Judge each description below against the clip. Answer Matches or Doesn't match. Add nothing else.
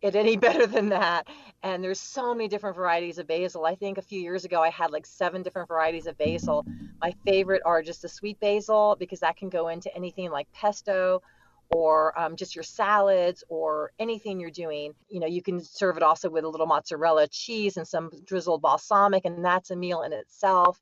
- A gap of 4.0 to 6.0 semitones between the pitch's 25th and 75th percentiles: Doesn't match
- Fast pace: Matches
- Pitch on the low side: Doesn't match